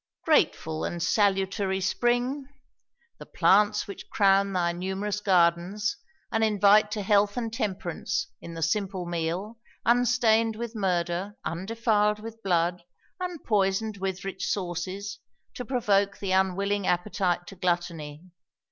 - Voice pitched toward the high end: Yes, high, 200 Hz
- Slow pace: Yes, slow, 120 wpm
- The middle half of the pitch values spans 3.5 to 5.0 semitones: No, average, 2.9 semitones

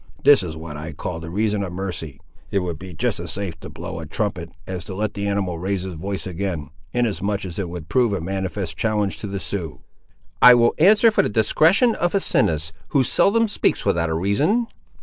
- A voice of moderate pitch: No, very low, 95 Hz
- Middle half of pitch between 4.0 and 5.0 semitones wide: Yes, average, 4.3 semitones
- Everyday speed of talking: No, fast, 210 wpm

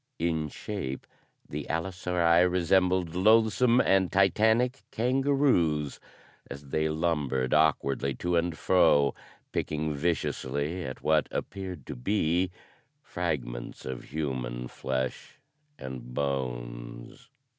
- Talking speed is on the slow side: Yes, slow, 100 wpm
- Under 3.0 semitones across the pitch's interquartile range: No, wide, 5.5 semitones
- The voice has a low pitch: Yes, very low, 80 Hz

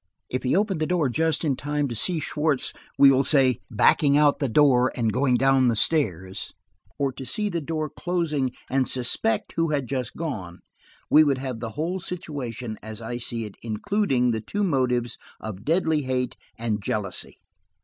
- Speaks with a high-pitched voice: No, low, 135 Hz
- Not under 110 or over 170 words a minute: No, average, 180 wpm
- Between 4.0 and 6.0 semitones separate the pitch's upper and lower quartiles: Yes, average, 4.7 semitones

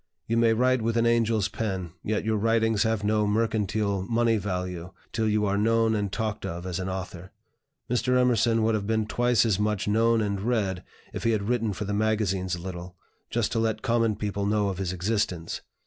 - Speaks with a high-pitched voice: No, low, 105 Hz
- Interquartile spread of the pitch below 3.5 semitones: Yes, narrow, 2.6 semitones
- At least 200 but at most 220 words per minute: Yes, fast, 205 wpm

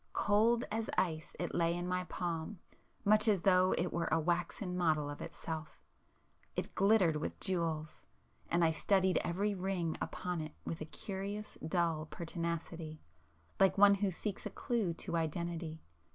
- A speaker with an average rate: Yes, average, 150 wpm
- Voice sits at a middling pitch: Yes, medium, 175 Hz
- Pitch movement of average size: Yes, average, 3.1 semitones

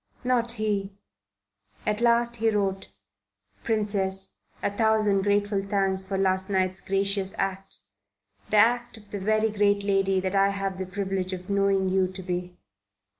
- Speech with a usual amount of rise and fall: No, narrow, 1.7 semitones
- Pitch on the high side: Yes, high, 195 Hz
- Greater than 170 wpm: No, average, 150 wpm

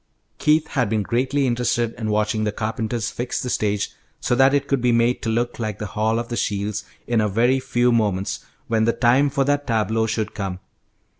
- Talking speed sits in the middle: No, fast, 210 wpm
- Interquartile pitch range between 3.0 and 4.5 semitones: No, narrow, 2.4 semitones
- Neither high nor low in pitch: No, low, 115 Hz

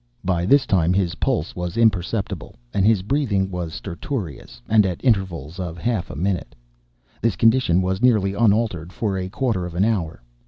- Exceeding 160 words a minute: Yes, average, 170 wpm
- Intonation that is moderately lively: Yes, average, 4.2 semitones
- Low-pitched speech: Yes, very low, 95 Hz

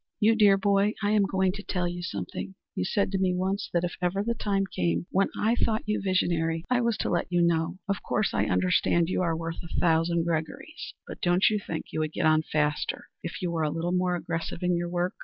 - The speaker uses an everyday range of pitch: Yes, average, 3.2 semitones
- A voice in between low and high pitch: Yes, medium, 175 Hz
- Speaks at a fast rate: Yes, fast, 240 wpm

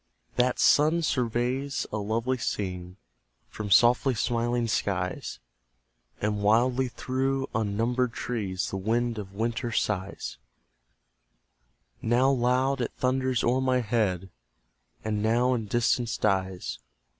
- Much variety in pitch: No, average, 3.4 semitones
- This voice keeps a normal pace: No, slow, 110 wpm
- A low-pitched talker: Yes, low, 120 Hz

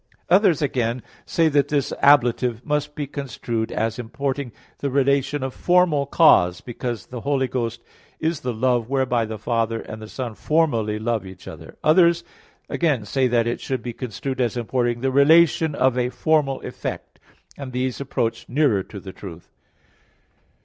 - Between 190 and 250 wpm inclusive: No, average, 165 wpm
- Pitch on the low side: Yes, low, 130 Hz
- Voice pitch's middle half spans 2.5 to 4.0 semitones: Yes, average, 3.6 semitones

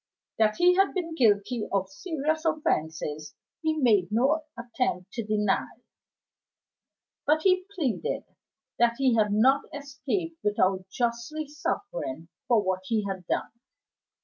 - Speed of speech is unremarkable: No, slow, 125 wpm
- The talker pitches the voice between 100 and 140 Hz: No, high, 235 Hz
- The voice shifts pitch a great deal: Yes, wide, 7.5 semitones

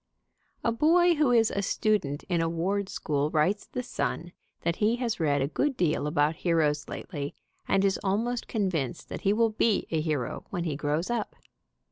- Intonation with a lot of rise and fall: Yes, wide, 6.5 semitones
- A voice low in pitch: No, medium, 185 Hz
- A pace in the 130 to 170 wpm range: No, average, 185 wpm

